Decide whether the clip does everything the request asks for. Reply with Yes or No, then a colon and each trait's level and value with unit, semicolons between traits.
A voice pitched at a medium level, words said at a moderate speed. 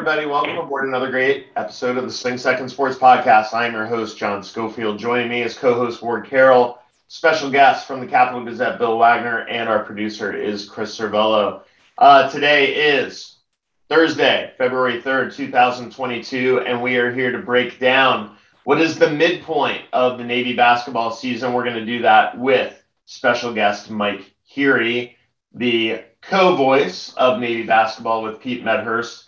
No: low, 120 Hz; average, 160 wpm